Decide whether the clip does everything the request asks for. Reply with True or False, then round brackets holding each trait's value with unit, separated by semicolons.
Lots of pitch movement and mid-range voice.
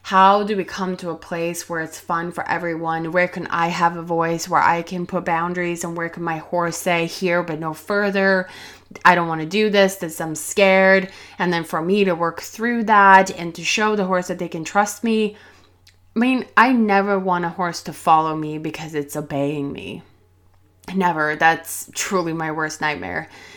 False (2.8 semitones; 170 Hz)